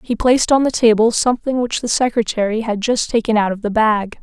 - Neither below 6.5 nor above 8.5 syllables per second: No, 5.9 syllables/s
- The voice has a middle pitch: No, high, 225 Hz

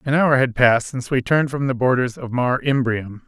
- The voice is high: No, low, 130 Hz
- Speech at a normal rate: No, fast, 240 wpm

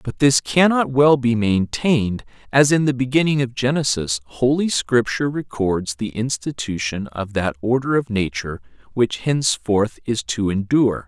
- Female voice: No, male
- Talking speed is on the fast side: No, average, 145 wpm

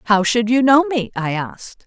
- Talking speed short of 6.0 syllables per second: Yes, 4.9 syllables/s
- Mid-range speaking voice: No, high, 225 Hz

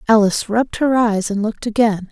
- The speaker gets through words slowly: No, average, 200 wpm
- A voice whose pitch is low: No, high, 220 Hz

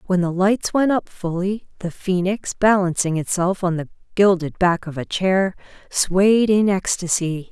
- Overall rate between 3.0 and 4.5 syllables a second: Yes, 4.2 syllables/s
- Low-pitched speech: No, medium, 185 Hz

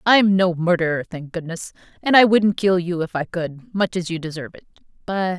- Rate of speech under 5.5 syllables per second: Yes, 5.1 syllables/s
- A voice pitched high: No, medium, 180 Hz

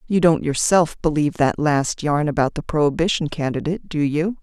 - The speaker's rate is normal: Yes, average, 175 wpm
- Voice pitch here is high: No, medium, 155 Hz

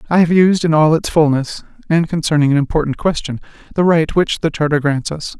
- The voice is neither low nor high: Yes, medium, 155 Hz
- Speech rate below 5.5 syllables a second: No, 5.7 syllables/s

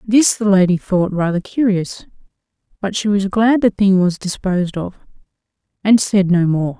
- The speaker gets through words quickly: No, average, 170 wpm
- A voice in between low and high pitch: No, high, 195 Hz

